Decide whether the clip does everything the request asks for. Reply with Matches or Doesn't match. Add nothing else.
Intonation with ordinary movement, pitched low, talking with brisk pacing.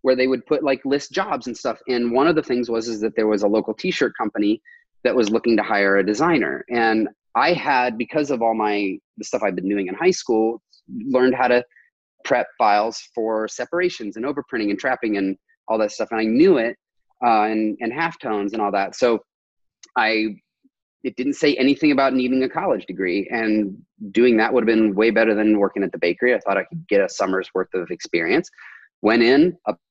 Matches